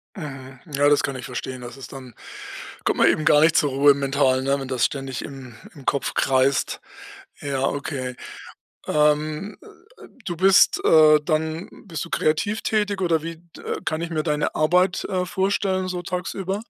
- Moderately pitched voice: Yes, medium, 150 Hz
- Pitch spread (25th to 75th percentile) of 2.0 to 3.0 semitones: No, average, 4.5 semitones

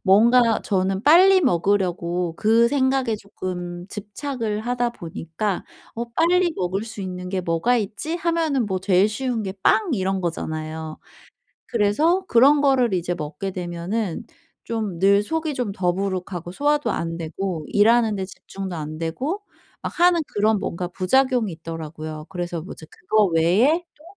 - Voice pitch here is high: Yes, high, 200 Hz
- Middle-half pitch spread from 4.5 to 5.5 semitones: No, wide, 5.9 semitones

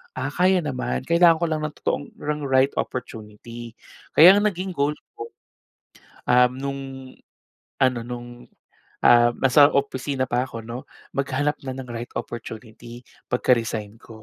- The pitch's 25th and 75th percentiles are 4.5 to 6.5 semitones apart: No, average, 3.7 semitones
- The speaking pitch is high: No, low, 130 Hz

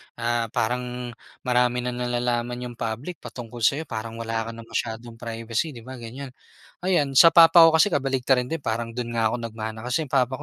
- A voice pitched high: No, low, 120 Hz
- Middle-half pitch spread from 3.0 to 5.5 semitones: No, narrow, 2.4 semitones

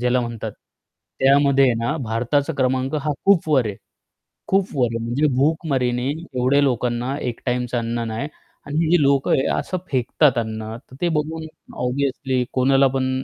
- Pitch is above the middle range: No, low, 130 Hz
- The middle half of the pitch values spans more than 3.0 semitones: No, average, 2.7 semitones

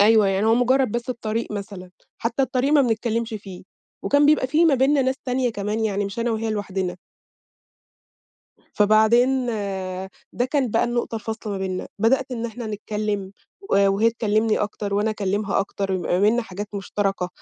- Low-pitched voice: No, high, 220 Hz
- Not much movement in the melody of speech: No, average, 3.1 semitones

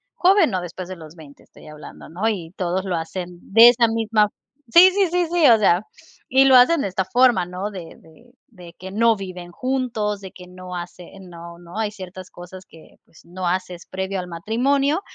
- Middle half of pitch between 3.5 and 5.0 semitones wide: Yes, average, 4.6 semitones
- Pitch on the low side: No, high, 190 Hz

